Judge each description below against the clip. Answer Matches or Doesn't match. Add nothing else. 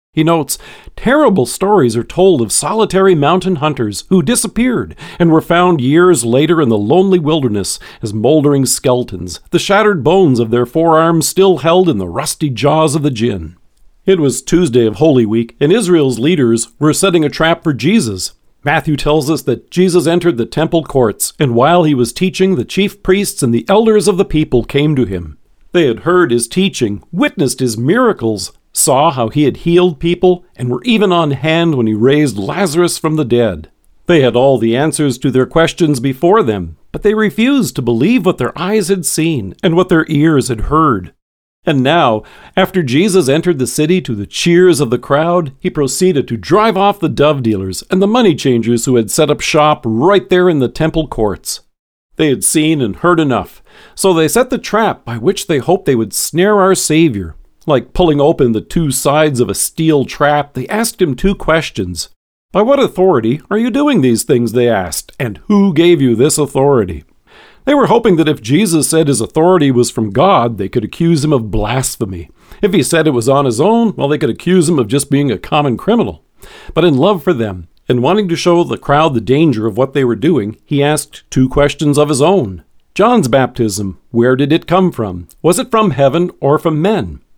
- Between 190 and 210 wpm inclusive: Matches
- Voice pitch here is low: Doesn't match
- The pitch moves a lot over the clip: Matches